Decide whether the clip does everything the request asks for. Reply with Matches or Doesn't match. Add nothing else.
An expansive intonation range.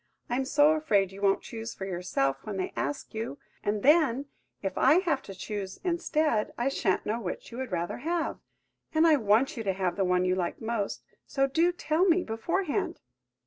Matches